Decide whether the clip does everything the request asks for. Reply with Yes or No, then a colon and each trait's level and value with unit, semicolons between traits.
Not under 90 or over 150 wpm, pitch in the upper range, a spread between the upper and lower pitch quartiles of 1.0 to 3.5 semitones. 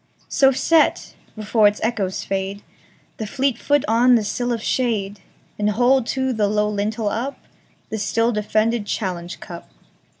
Yes: slow, 135 wpm; high, 220 Hz; average, 2.9 semitones